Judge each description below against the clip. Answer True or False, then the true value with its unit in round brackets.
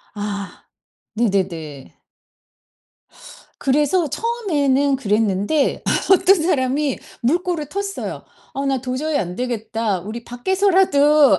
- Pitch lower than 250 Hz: False (270 Hz)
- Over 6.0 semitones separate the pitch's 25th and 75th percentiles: True (6.6 semitones)